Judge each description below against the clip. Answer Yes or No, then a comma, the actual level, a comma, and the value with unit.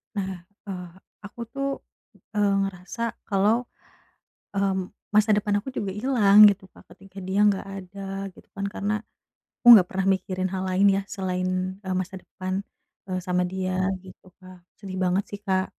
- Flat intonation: Yes, narrow, 1.5 semitones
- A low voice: No, high, 195 Hz